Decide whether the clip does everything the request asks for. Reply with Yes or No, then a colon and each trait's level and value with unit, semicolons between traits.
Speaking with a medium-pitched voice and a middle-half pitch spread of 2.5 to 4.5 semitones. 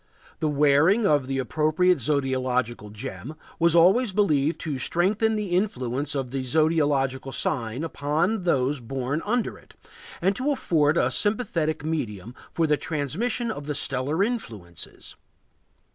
No: medium, 150 Hz; average, 5.2 semitones